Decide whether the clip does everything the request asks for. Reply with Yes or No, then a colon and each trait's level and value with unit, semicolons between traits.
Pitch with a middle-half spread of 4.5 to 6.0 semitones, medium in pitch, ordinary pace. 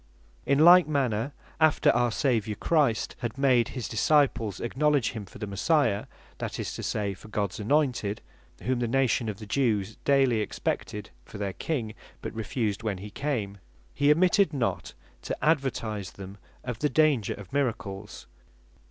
No: average, 5.1 semitones; low, 120 Hz; average, 160 wpm